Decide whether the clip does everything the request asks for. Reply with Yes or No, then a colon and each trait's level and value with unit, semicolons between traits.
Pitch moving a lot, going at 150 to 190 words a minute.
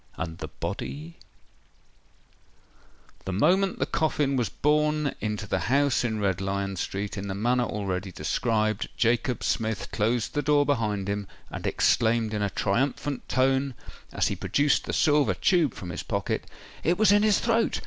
Yes: wide, 6.3 semitones; average, 160 wpm